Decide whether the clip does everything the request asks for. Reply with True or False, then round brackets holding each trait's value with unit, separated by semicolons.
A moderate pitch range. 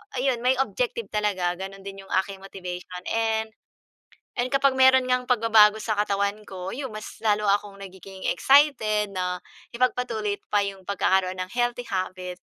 True (4.1 semitones)